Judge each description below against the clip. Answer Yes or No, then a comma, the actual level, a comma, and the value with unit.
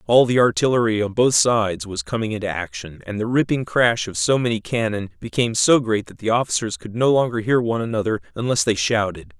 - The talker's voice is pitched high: No, low, 110 Hz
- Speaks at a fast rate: Yes, fast, 210 wpm